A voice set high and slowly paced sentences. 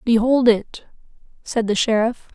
Yes: high, 230 Hz; slow, 130 wpm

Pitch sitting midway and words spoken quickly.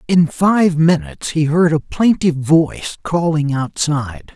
No: medium, 160 Hz; average, 140 wpm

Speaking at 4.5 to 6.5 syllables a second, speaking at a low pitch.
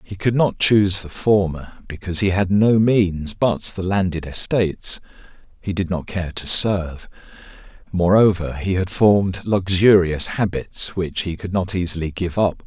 No: 4.3 syllables/s; very low, 95 Hz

